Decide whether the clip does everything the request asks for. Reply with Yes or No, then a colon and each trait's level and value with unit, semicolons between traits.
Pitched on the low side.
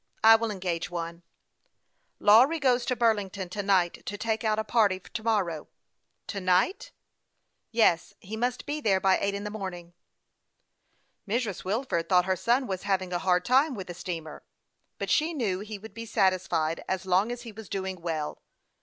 No: high, 200 Hz